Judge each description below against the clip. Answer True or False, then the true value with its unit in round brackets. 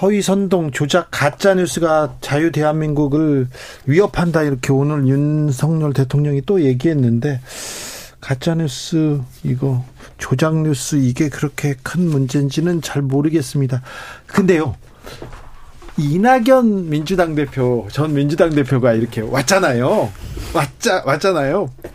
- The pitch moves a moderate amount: True (3.4 semitones)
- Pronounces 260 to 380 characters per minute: True (270 characters per minute)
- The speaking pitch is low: False (145 Hz)